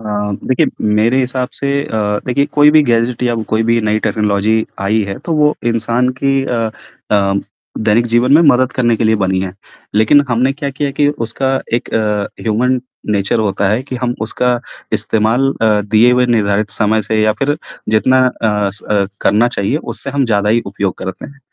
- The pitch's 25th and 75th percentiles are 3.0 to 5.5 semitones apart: Yes, average, 3.3 semitones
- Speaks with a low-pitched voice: Yes, low, 115 Hz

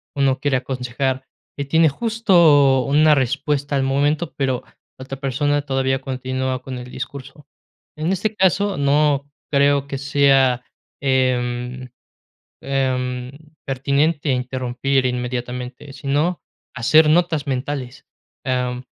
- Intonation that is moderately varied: No, narrow, 2.1 semitones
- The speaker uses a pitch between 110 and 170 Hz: Yes, low, 135 Hz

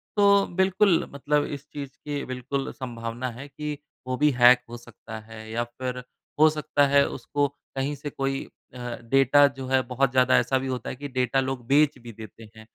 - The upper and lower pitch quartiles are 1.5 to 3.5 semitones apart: Yes, average, 2.8 semitones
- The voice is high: No, low, 135 Hz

